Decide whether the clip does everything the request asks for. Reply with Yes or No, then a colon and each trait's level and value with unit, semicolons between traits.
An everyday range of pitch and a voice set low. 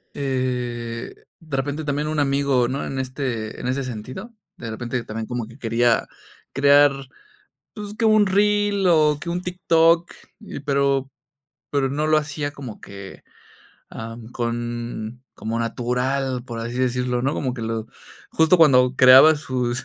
Yes: average, 3.7 semitones; low, 130 Hz